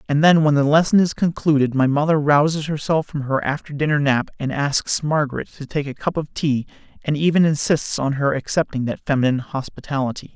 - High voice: No, medium, 145 Hz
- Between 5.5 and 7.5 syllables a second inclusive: Yes, 5.7 syllables/s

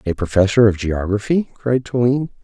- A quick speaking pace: No, average, 150 wpm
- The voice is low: Yes, low, 110 Hz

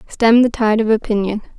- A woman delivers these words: Yes, female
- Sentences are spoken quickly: No, average, 190 wpm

